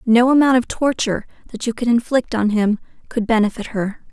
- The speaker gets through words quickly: No, average, 190 wpm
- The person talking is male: No, female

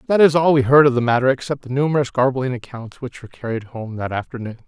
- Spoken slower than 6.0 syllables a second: No, 6.6 syllables/s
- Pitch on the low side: Yes, low, 130 Hz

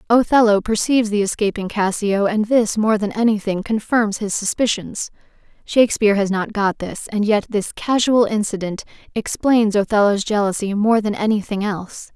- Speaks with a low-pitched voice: No, high, 210 Hz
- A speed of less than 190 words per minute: Yes, average, 150 wpm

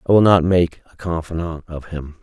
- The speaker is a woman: No, male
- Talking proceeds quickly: Yes, fast, 215 wpm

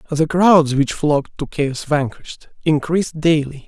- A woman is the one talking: No, male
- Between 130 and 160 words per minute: Yes, average, 145 wpm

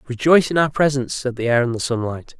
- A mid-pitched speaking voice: No, low, 130 Hz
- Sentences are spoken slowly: No, fast, 250 wpm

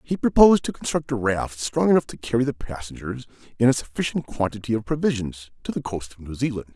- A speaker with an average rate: No, fast, 215 wpm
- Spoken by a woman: No, male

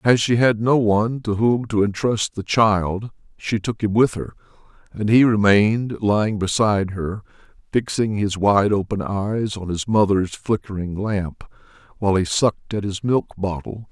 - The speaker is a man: Yes, male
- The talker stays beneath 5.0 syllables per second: Yes, 4.5 syllables/s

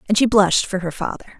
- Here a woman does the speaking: Yes, female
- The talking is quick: Yes, fast, 260 wpm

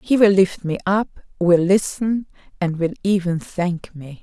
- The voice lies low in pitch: No, medium, 185 Hz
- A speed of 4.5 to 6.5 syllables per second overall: No, 4.1 syllables/s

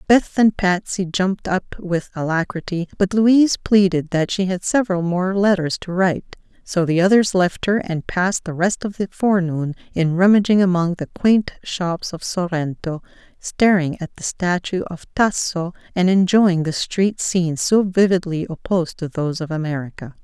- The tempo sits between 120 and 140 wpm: No, average, 165 wpm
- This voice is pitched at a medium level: Yes, medium, 180 Hz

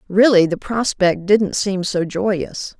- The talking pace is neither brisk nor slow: Yes, average, 150 wpm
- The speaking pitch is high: Yes, high, 195 Hz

